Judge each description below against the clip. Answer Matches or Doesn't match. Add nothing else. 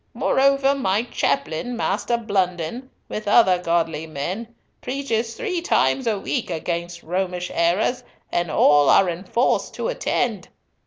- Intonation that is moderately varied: Doesn't match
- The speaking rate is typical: Doesn't match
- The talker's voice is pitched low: Doesn't match